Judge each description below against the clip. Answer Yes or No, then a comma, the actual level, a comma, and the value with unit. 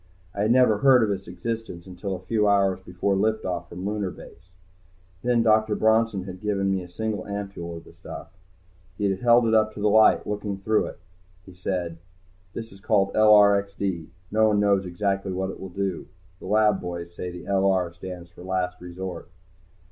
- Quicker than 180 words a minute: Yes, average, 195 wpm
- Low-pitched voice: Yes, low, 100 Hz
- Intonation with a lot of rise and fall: No, average, 2.8 semitones